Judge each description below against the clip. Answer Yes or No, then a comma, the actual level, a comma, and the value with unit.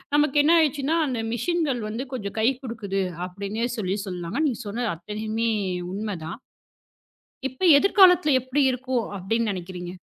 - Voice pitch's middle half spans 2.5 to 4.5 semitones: No, average, 5.1 semitones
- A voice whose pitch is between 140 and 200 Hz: No, high, 230 Hz